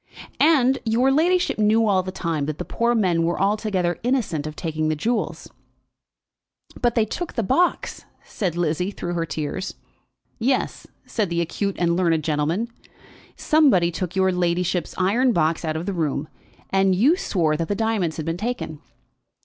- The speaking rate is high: No, average, 165 wpm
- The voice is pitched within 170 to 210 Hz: Yes, medium, 185 Hz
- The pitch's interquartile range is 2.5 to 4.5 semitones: No, wide, 5.4 semitones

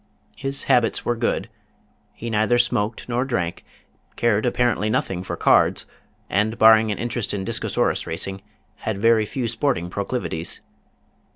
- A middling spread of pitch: Yes, average, 3.1 semitones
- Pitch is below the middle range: Yes, low, 110 Hz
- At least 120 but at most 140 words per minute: Yes, slow, 135 wpm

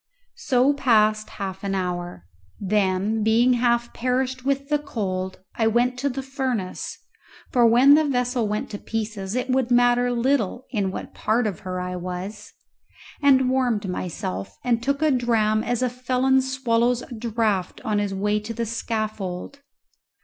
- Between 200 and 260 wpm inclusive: No, average, 160 wpm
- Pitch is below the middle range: No, high, 230 Hz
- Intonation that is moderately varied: Yes, average, 3.6 semitones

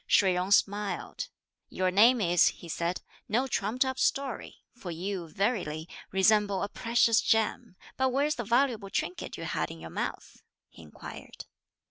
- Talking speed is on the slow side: No, average, 155 wpm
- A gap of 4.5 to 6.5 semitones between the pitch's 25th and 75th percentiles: Yes, average, 4.8 semitones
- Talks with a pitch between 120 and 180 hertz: No, high, 205 Hz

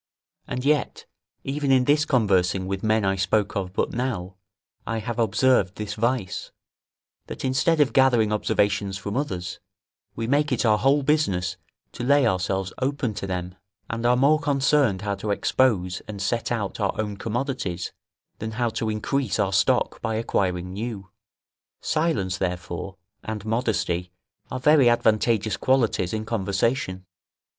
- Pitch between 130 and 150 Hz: No, low, 110 Hz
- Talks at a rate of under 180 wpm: Yes, average, 150 wpm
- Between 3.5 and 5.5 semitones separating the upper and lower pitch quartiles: Yes, average, 5.0 semitones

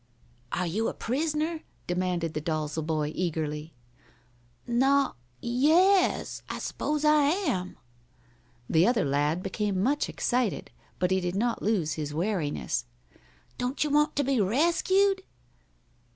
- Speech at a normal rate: No, slow, 130 wpm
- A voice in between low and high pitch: No, high, 215 Hz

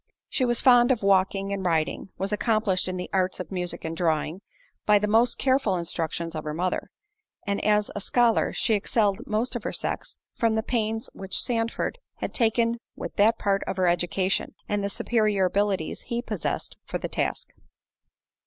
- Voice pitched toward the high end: Yes, high, 205 Hz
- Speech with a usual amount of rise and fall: Yes, average, 3.7 semitones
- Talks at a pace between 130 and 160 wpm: No, average, 175 wpm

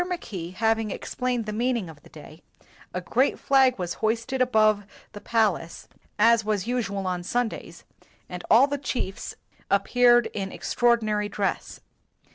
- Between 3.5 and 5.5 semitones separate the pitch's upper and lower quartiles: Yes, average, 3.8 semitones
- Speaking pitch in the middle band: No, high, 220 Hz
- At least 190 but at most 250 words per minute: No, average, 145 wpm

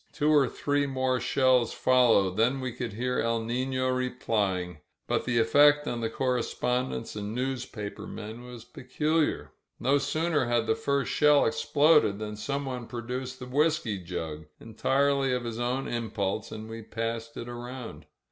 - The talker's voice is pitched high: No, low, 125 Hz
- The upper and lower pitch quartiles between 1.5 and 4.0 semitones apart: Yes, average, 2.9 semitones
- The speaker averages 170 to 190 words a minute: No, average, 155 wpm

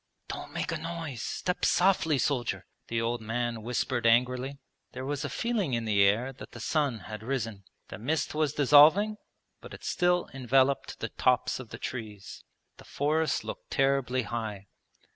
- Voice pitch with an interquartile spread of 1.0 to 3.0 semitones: No, average, 4.4 semitones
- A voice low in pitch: Yes, low, 130 Hz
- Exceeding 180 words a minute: No, average, 165 wpm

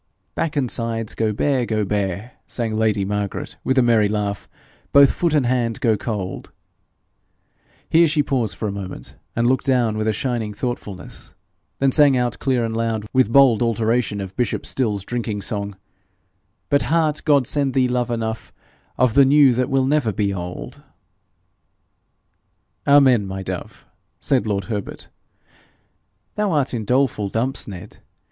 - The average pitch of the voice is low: Yes, low, 115 Hz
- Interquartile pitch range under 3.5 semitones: No, average, 4.1 semitones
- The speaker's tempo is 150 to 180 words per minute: Yes, average, 155 wpm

